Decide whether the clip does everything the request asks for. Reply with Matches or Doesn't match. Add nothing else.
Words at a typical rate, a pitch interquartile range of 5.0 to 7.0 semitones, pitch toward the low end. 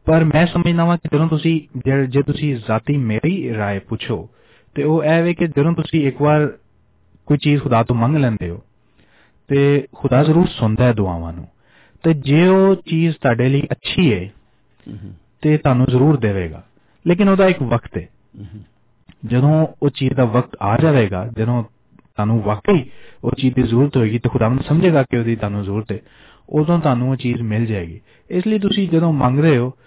Matches